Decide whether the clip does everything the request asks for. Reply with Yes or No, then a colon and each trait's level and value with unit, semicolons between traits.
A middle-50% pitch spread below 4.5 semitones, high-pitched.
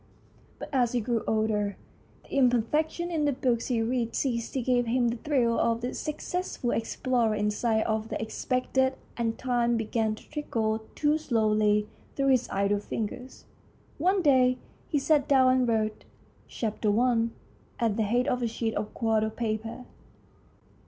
Yes: average, 2.8 semitones; high, 235 Hz